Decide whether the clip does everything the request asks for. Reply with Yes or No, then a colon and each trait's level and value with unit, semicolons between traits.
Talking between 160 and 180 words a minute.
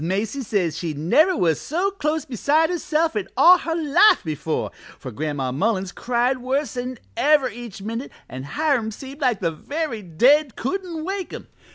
Yes: average, 170 wpm